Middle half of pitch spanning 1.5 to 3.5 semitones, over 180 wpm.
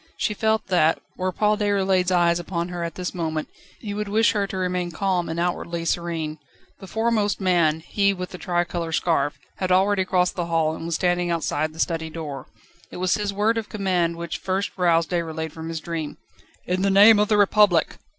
Yes: average, 3.0 semitones; average, 200 wpm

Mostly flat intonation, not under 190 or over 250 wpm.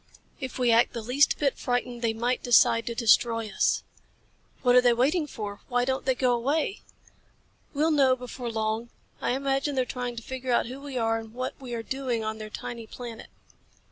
Yes: narrow, 2.3 semitones; average, 200 wpm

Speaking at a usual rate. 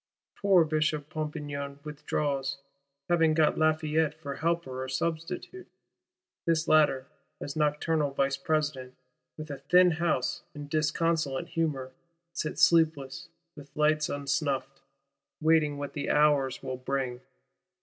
No: slow, 115 wpm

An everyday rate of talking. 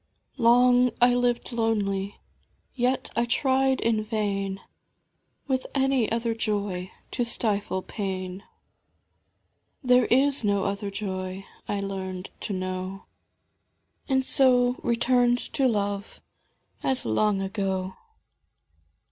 No: slow, 105 wpm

